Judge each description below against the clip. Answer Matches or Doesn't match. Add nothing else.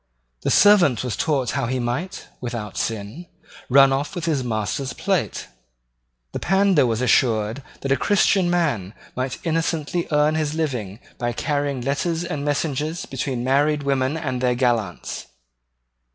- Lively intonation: Doesn't match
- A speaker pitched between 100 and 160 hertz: Matches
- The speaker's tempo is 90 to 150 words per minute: Matches